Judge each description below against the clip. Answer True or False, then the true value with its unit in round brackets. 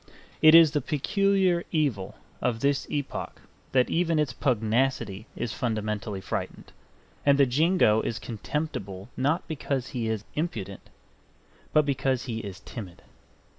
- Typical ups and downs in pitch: False (5.8 semitones)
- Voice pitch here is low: True (130 Hz)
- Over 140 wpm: False (135 wpm)